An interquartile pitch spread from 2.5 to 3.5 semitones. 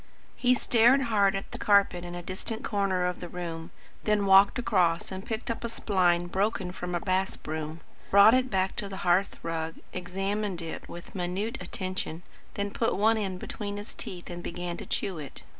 Yes: average, 2.9 semitones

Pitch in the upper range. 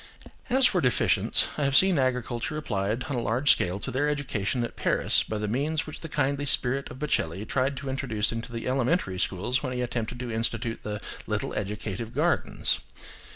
No: low, 125 Hz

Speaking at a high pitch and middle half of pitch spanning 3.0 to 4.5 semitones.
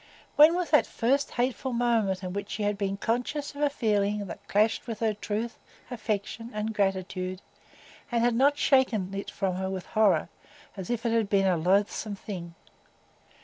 Yes: high, 210 Hz; average, 3.5 semitones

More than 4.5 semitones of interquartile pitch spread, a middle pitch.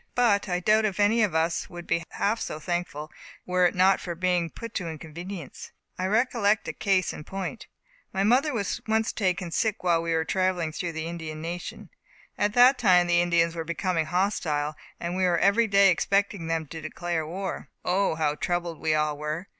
No: average, 3.3 semitones; medium, 180 Hz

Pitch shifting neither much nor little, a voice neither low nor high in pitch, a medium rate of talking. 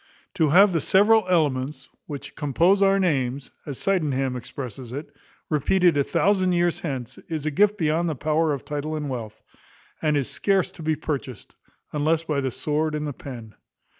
Yes: average, 4.0 semitones; medium, 150 Hz; average, 175 wpm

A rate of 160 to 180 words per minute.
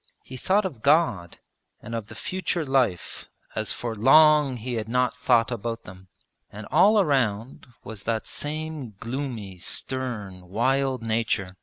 No: average, 145 wpm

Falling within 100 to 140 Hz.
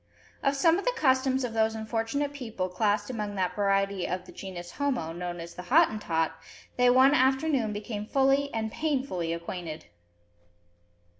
No: high, 220 Hz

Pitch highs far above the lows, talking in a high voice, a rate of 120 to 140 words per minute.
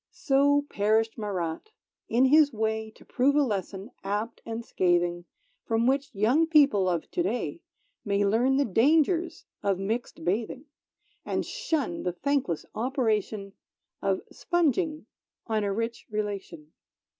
Yes: wide, 5.9 semitones; high, 225 Hz; slow, 135 wpm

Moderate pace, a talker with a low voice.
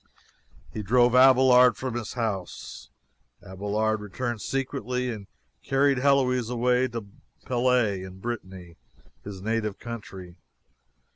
No: slow, 110 wpm; low, 120 Hz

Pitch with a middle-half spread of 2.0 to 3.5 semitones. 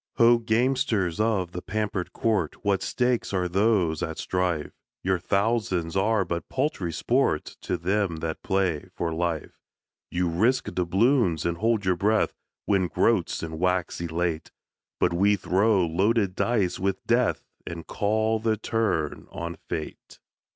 No: average, 4.3 semitones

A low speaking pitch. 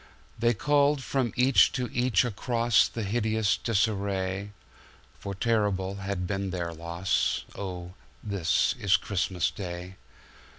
Yes: low, 100 Hz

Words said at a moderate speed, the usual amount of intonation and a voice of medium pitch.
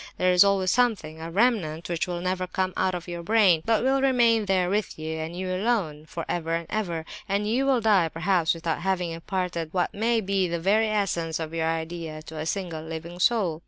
No: fast, 220 wpm; average, 3.7 semitones; medium, 180 Hz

